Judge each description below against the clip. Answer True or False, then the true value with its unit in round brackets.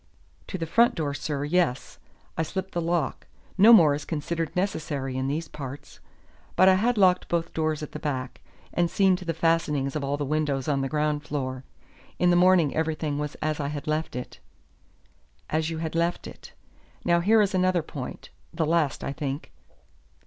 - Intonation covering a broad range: False (3.2 semitones)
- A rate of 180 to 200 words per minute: True (190 wpm)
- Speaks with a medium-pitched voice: True (155 Hz)